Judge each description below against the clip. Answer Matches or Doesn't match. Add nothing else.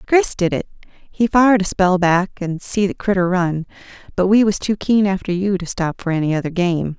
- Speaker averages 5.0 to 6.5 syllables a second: Matches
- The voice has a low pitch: Doesn't match